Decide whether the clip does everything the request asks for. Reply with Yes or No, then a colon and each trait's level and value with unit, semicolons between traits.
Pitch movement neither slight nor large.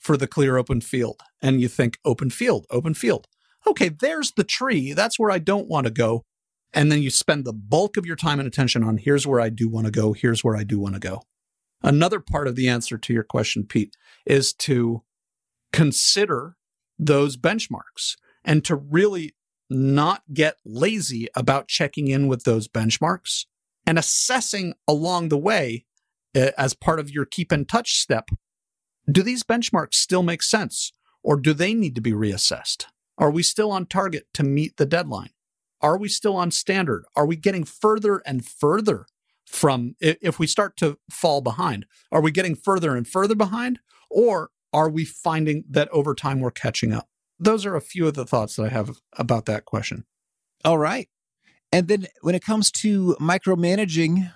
No: wide, 6.8 semitones